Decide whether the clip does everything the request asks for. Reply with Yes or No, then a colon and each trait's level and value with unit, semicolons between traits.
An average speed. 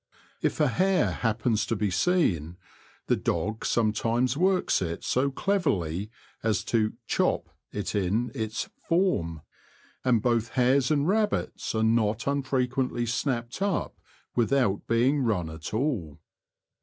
No: slow, 130 wpm